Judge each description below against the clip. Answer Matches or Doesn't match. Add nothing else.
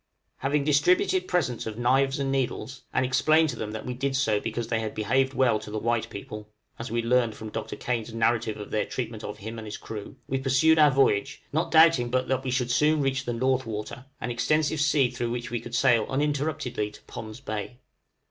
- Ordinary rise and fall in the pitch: Matches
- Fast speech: Matches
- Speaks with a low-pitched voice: Matches